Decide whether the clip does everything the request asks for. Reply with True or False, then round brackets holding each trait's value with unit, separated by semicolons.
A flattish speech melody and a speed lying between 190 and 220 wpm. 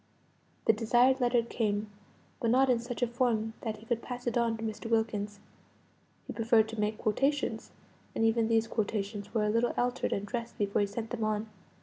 True (2.0 semitones; 200 wpm)